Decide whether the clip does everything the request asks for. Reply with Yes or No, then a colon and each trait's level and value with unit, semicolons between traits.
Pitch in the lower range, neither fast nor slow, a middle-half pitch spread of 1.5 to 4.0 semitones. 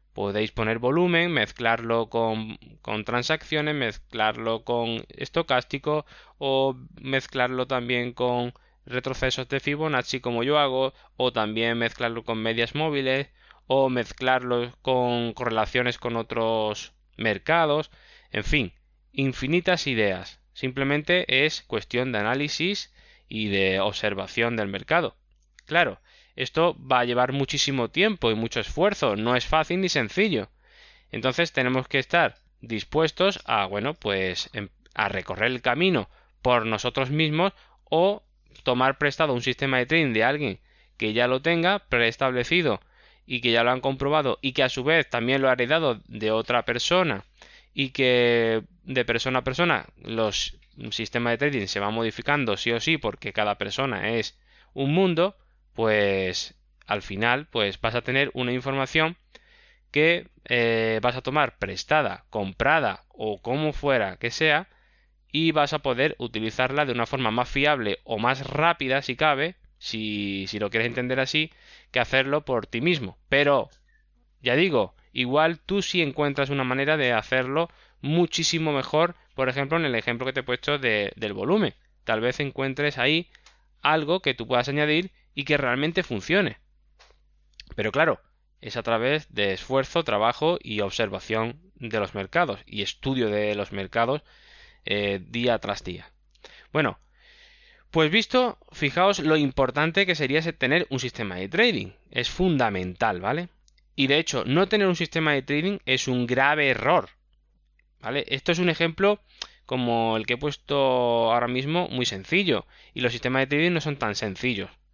No: low, 130 Hz; average, 150 wpm; average, 4.8 semitones